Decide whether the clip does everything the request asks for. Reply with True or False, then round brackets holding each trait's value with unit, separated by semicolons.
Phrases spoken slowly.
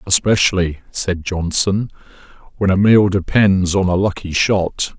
True (130 wpm)